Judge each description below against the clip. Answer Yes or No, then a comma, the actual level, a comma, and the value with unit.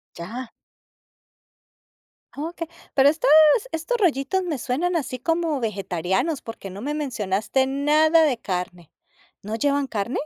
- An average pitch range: No, wide, 6.7 semitones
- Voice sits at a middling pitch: No, very high, 270 Hz